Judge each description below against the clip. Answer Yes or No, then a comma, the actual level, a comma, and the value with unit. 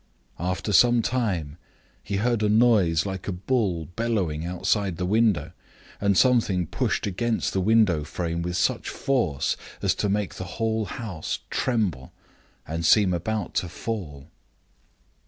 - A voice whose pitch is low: Yes, very low, 95 Hz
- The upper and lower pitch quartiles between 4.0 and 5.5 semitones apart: Yes, average, 4.4 semitones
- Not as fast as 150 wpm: Yes, average, 140 wpm